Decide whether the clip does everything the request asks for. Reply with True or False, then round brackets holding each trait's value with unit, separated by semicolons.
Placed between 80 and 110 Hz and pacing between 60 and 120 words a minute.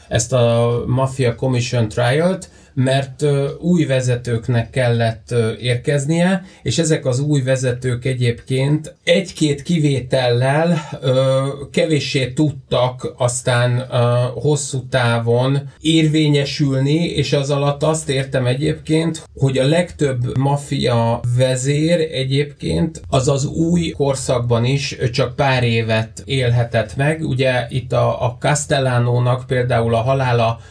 False (135 Hz; 110 wpm)